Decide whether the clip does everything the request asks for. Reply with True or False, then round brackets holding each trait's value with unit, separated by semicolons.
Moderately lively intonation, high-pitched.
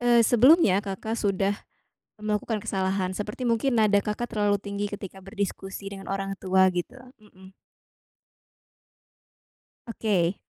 False (2.2 semitones; 205 Hz)